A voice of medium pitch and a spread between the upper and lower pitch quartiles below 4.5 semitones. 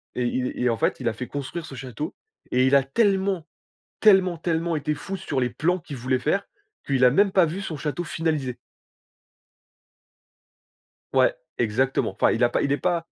No: medium, 150 Hz; average, 5.3 semitones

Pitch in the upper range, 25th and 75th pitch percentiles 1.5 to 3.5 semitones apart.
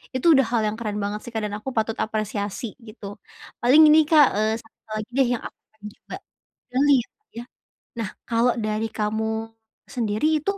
Yes: high, 225 Hz; average, 3.0 semitones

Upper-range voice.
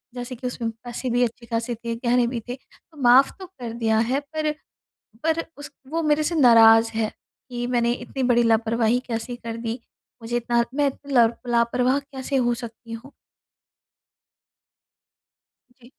Yes: high, 240 Hz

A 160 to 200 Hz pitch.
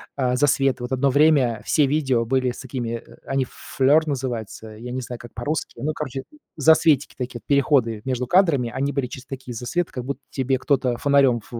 No: low, 130 Hz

